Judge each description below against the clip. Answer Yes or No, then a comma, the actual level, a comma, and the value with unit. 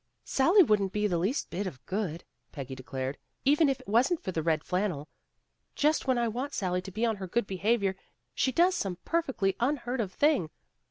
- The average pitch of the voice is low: No, high, 210 Hz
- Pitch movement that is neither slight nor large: No, wide, 6.6 semitones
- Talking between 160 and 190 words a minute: No, fast, 205 wpm